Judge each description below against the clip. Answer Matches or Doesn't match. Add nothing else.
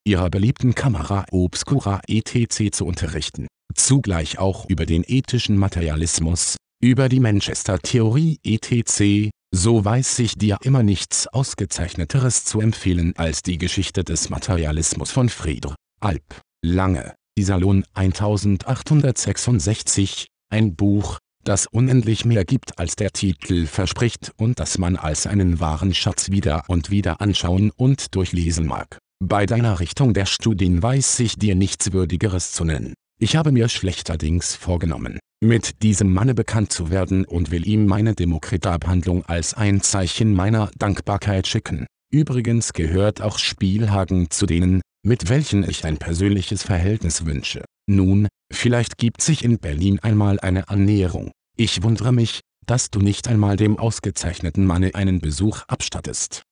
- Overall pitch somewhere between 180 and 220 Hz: Doesn't match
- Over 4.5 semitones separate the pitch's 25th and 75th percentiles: Doesn't match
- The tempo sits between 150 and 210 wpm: Doesn't match